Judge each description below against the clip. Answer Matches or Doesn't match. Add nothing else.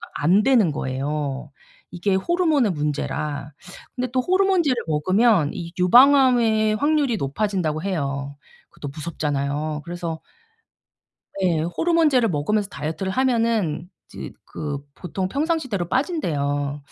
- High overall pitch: Doesn't match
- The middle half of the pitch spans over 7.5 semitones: Matches